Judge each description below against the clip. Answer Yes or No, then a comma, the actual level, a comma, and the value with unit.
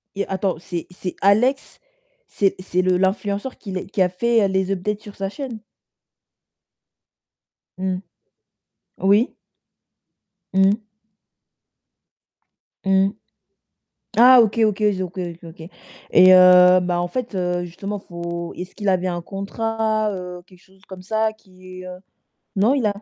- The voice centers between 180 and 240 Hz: Yes, high, 190 Hz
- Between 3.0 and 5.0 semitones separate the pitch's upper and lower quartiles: No, narrow, 2.5 semitones